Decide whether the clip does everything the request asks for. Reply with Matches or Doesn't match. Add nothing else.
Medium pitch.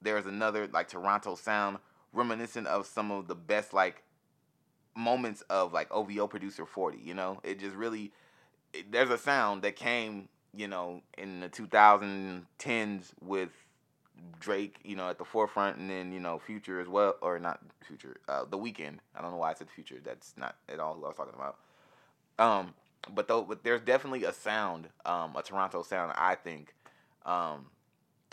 Doesn't match